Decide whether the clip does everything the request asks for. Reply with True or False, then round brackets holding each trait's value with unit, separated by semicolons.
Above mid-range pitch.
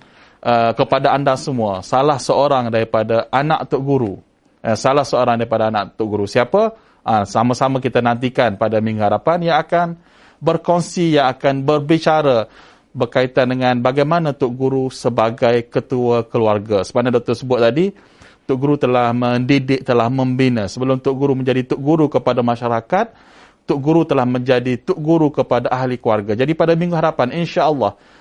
False (130 Hz)